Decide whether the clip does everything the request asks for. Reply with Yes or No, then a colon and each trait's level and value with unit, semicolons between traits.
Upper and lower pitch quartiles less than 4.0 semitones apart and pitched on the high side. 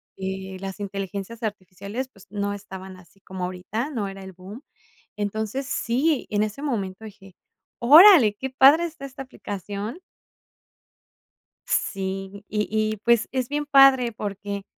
No: average, 4.8 semitones; high, 210 Hz